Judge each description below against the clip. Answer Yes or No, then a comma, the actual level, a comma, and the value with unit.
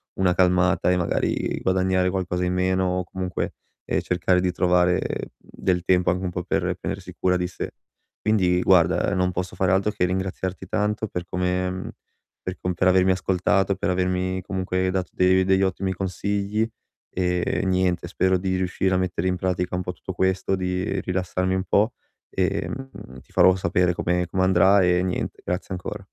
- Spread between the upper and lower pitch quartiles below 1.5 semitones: Yes, narrow, 0.7 semitones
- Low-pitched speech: Yes, very low, 90 Hz